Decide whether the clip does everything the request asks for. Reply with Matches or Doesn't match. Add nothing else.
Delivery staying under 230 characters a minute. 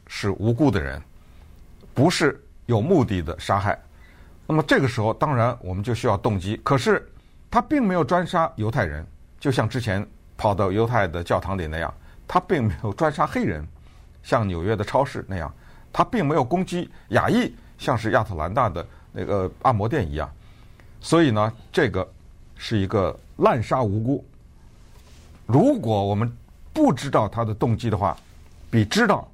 Doesn't match